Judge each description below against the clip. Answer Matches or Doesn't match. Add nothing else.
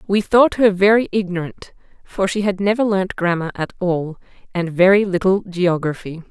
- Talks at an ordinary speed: Matches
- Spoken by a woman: Matches